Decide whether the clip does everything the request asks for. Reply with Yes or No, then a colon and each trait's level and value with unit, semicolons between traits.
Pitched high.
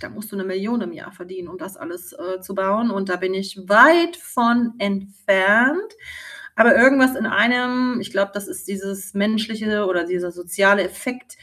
Yes: high, 200 Hz